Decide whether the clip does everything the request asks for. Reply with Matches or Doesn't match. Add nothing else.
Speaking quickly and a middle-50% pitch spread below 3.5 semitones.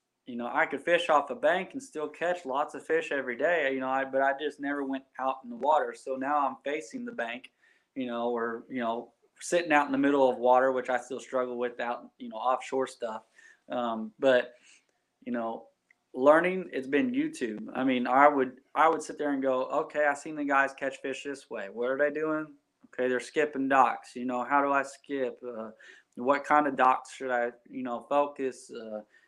Matches